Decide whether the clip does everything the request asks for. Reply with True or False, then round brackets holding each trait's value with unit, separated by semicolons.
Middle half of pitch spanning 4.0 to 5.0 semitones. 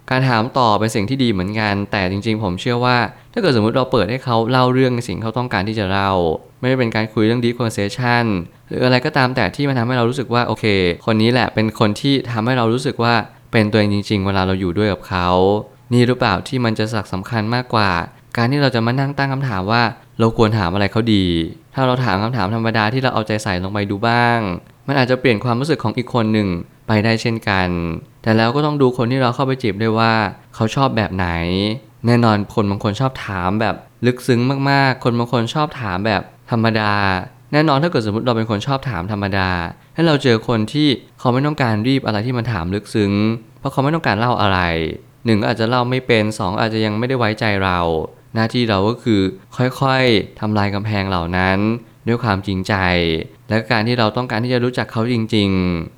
False (3.4 semitones)